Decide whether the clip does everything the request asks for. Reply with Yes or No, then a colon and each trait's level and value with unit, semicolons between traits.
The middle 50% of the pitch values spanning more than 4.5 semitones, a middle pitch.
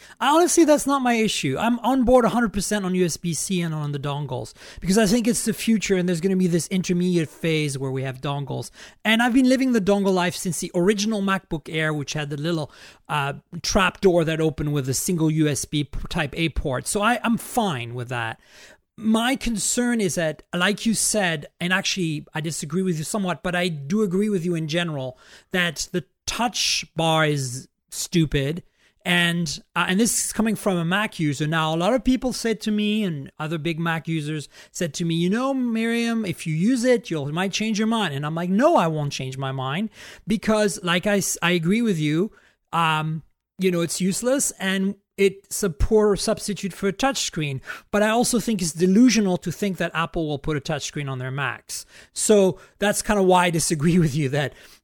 Yes: average, 5.1 semitones; medium, 180 Hz